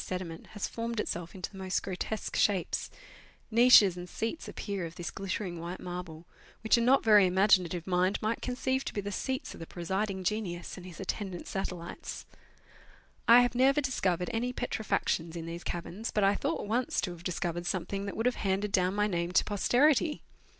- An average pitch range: Yes, average, 4.1 semitones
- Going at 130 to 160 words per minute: No, average, 190 wpm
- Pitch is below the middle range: No, high, 195 Hz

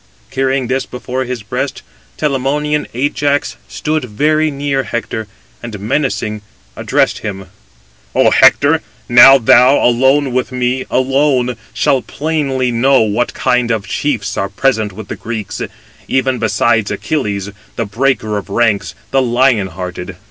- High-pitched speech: No, low, 125 Hz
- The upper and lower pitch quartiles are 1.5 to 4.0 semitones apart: Yes, average, 3.7 semitones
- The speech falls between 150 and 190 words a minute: No, slow, 135 wpm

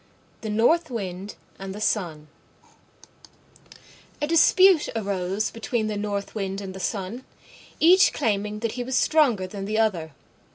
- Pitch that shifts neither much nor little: Yes, average, 3.7 semitones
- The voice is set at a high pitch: Yes, high, 210 Hz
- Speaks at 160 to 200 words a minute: No, average, 140 wpm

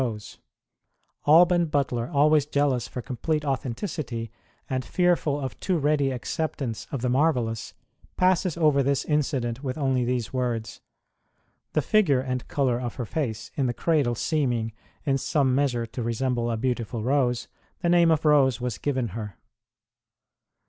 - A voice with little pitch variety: No, average, 3.8 semitones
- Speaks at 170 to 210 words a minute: No, average, 155 wpm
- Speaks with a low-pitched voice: Yes, low, 130 Hz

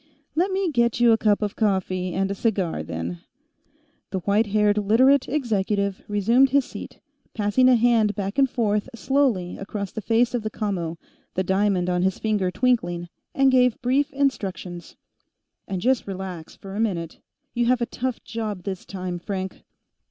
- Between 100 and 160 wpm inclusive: No, average, 170 wpm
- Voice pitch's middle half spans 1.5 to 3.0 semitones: No, average, 4.3 semitones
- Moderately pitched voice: No, high, 210 Hz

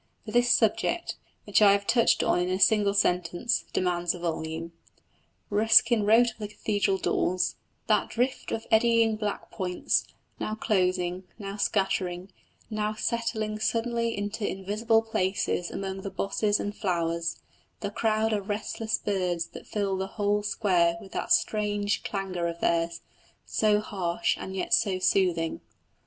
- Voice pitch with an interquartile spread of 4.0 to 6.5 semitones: No, average, 3.0 semitones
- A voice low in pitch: No, high, 205 Hz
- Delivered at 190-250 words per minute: No, average, 145 wpm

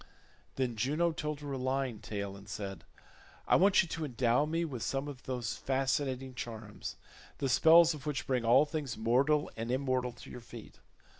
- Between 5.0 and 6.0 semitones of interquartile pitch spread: No, average, 3.9 semitones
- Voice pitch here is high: No, low, 130 Hz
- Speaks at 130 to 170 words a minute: No, average, 180 wpm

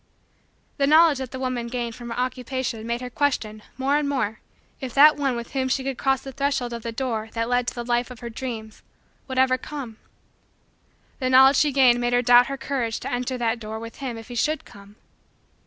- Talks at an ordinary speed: No, fast, 220 wpm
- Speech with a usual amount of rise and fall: No, narrow, 2.3 semitones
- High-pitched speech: Yes, very high, 250 Hz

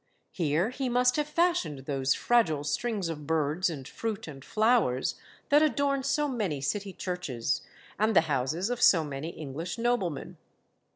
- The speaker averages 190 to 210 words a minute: No, average, 155 wpm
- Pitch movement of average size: No, wide, 8.7 semitones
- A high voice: No, medium, 180 Hz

